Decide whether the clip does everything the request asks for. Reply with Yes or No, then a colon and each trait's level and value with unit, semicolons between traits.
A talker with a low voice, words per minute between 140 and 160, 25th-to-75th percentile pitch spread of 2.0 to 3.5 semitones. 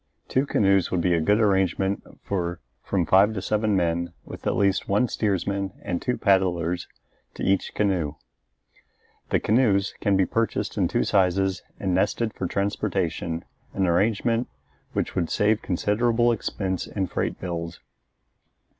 Yes: very low, 95 Hz; average, 145 wpm; average, 2.7 semitones